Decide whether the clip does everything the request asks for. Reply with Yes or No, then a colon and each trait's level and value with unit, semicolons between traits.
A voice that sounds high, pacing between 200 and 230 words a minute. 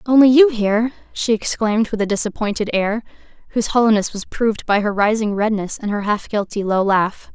No: high, 215 Hz; average, 190 wpm